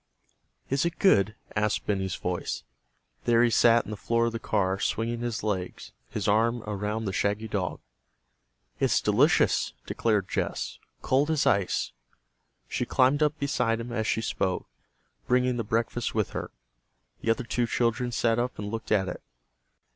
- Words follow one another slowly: No, average, 160 wpm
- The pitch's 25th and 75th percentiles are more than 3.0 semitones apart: No, average, 2.7 semitones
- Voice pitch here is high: No, low, 115 Hz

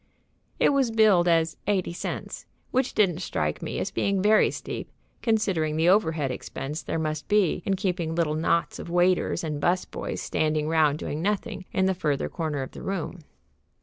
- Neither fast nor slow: Yes, average, 180 wpm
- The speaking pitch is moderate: Yes, medium, 170 Hz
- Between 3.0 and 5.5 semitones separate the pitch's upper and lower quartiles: Yes, average, 3.9 semitones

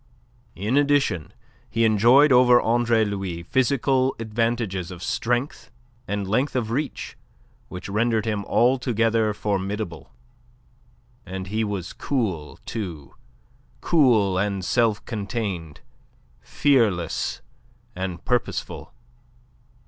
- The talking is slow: Yes, slow, 95 wpm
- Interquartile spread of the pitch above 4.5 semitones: No, average, 4.2 semitones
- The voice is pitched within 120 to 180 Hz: No, low, 110 Hz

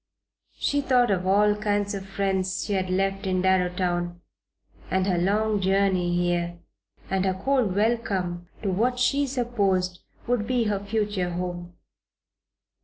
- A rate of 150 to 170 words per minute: No, average, 140 wpm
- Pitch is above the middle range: Yes, high, 195 Hz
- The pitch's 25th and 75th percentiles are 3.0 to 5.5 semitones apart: No, narrow, 2.6 semitones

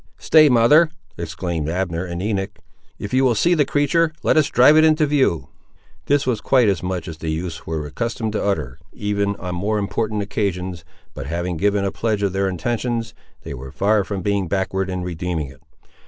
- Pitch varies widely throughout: No, average, 4.9 semitones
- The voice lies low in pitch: Yes, low, 100 Hz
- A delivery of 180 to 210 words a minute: Yes, average, 195 wpm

